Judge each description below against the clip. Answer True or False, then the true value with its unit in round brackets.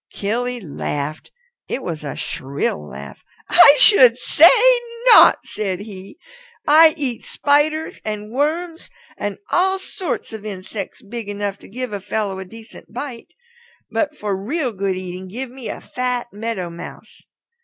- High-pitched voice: True (220 Hz)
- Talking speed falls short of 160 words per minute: True (145 wpm)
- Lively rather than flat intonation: True (5.8 semitones)